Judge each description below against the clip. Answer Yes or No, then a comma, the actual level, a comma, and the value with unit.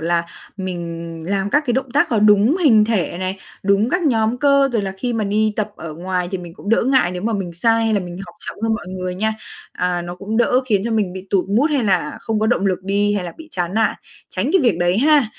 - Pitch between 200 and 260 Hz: Yes, high, 205 Hz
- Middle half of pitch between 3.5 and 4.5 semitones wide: Yes, average, 4.0 semitones